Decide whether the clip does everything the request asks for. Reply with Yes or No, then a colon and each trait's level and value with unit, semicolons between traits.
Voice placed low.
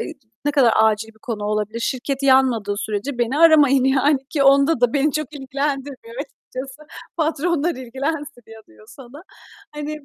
No: very high, 270 Hz